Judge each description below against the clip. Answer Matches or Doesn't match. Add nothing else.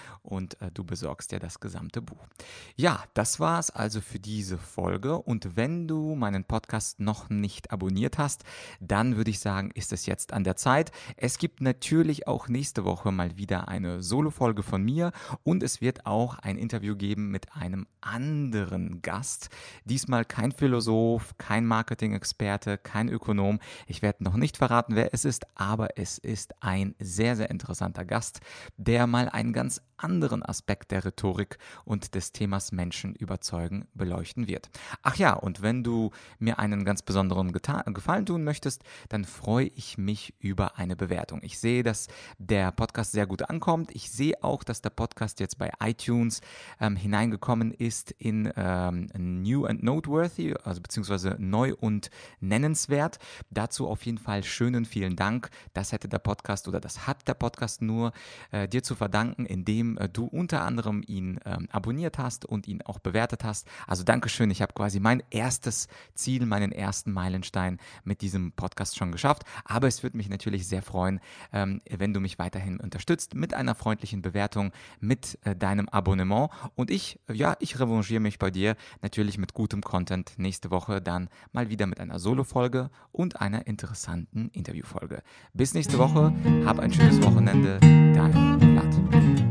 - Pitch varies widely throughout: Doesn't match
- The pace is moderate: Matches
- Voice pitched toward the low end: Matches